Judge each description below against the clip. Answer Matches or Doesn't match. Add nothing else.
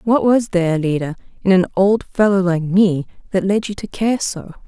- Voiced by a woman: Matches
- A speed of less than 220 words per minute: Matches